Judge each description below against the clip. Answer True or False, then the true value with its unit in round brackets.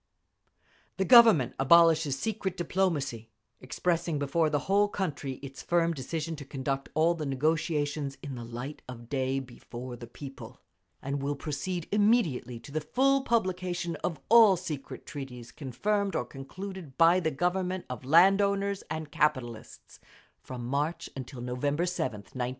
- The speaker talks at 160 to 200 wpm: False (145 wpm)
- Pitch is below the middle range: False (150 Hz)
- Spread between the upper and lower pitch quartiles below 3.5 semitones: False (5.1 semitones)